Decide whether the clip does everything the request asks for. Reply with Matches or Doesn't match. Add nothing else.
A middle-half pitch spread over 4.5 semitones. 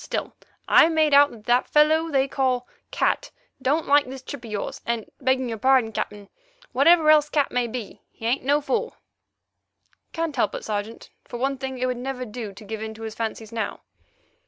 Doesn't match